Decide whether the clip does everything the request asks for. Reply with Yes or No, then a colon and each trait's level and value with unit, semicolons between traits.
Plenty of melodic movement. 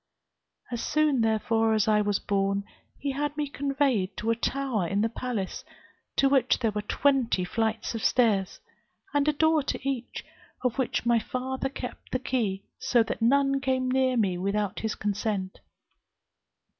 No: average, 4.3 semitones